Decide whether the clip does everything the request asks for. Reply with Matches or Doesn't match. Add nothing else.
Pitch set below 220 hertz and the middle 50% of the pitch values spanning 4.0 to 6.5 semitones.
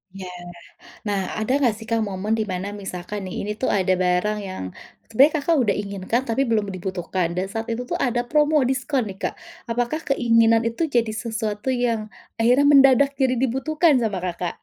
Doesn't match